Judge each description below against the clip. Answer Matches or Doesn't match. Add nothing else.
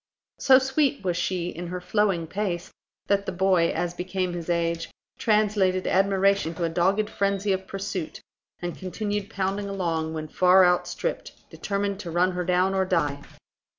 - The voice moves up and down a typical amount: Doesn't match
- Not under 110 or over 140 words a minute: Doesn't match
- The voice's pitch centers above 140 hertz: Matches